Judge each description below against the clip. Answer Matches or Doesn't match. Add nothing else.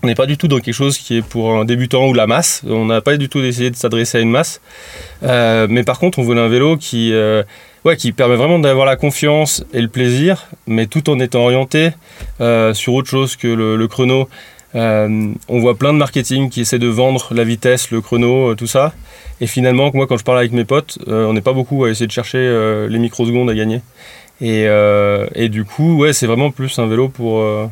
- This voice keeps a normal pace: Doesn't match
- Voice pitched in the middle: Doesn't match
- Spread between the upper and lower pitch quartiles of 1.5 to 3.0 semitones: Matches